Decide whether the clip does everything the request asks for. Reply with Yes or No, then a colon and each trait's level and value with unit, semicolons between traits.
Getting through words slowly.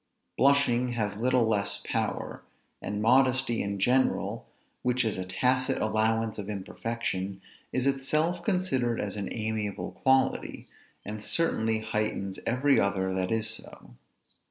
Yes: slow, 130 wpm